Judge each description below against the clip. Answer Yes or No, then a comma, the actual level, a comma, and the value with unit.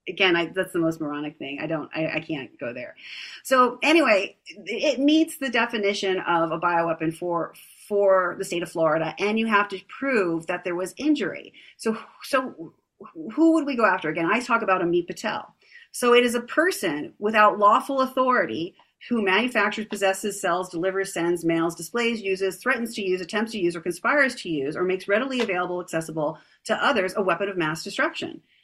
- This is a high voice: Yes, high, 195 Hz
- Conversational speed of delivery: Yes, average, 190 wpm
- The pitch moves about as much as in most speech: No, wide, 5.7 semitones